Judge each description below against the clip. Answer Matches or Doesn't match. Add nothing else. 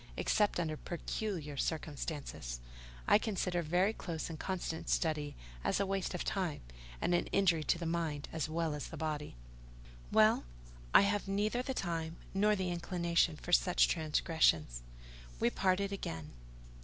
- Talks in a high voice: Doesn't match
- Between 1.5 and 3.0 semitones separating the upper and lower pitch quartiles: Doesn't match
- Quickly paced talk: Doesn't match